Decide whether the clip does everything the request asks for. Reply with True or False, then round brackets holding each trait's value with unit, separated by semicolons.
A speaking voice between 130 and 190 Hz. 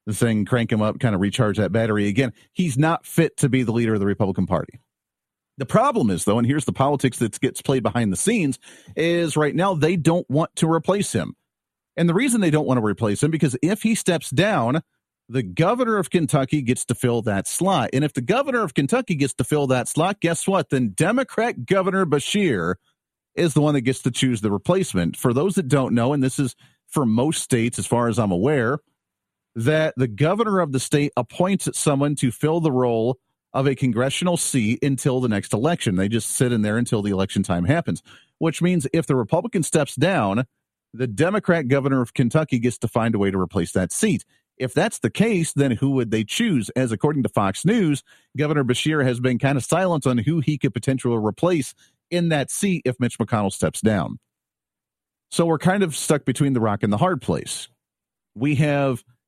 True (135 Hz)